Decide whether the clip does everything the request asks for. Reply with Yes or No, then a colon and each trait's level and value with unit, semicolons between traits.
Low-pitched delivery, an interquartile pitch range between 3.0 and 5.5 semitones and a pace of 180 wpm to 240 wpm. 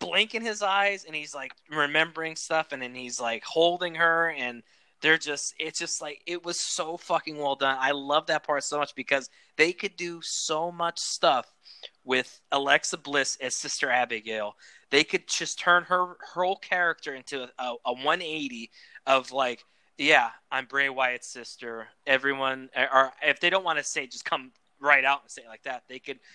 No: medium, 145 Hz; average, 4.0 semitones; average, 185 wpm